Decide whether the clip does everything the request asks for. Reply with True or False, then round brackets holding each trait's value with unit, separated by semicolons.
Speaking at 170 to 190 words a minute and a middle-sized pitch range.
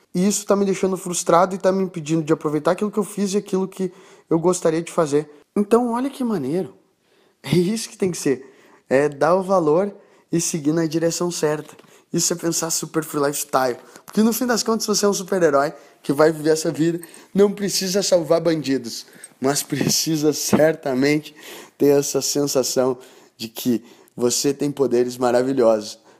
True (180 wpm; 4.9 semitones)